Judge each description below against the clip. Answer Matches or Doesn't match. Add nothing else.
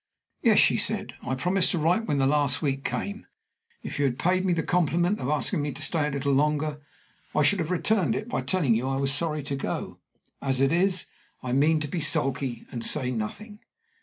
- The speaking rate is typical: Doesn't match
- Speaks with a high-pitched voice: Doesn't match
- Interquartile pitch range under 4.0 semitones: Doesn't match